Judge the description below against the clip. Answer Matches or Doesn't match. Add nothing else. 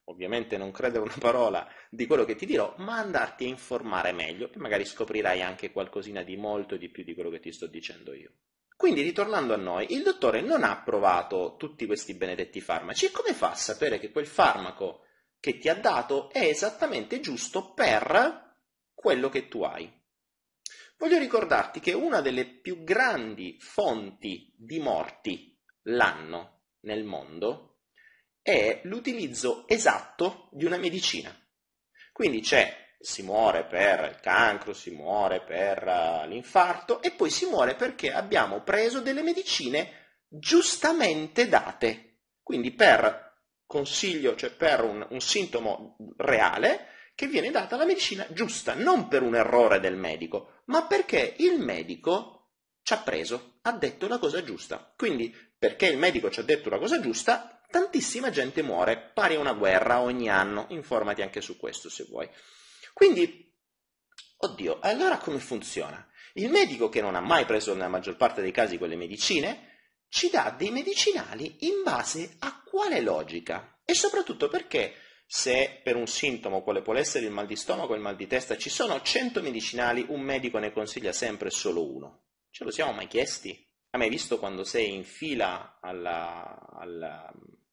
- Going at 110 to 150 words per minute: Doesn't match